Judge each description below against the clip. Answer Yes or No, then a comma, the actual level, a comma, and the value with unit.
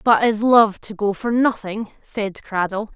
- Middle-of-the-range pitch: No, high, 215 Hz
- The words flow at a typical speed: Yes, average, 185 wpm